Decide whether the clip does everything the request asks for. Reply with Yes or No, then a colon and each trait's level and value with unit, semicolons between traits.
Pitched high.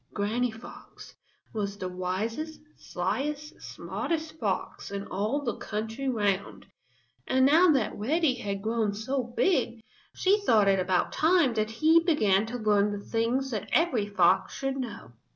Yes: high, 230 Hz